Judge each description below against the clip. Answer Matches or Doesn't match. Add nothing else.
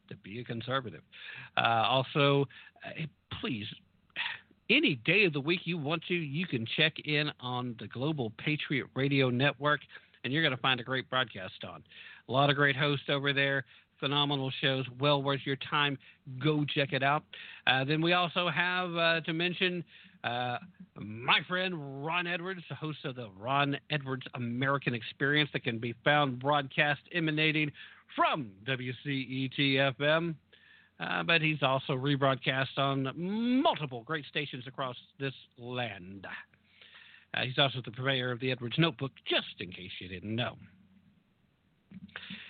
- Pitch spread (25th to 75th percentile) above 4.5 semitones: Doesn't match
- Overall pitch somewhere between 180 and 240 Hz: Doesn't match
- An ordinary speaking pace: Matches